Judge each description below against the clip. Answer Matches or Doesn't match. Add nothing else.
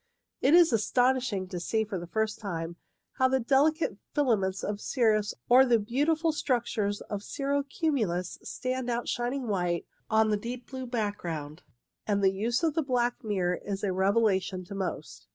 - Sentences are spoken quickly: Doesn't match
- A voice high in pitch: Matches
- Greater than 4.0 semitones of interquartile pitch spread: Matches